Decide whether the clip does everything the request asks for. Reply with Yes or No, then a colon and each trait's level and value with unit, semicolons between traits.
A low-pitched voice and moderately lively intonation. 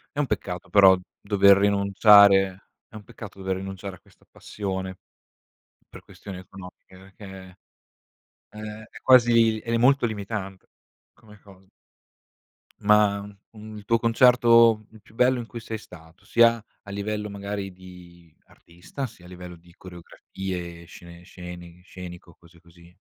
Yes: low, 100 Hz; average, 3.0 semitones